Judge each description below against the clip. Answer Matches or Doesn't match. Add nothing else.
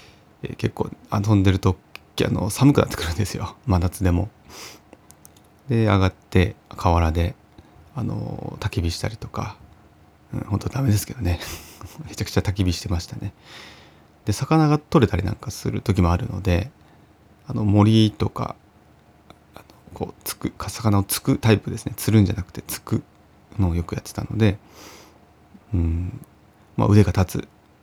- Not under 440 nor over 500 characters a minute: Doesn't match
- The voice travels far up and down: Doesn't match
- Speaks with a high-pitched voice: Doesn't match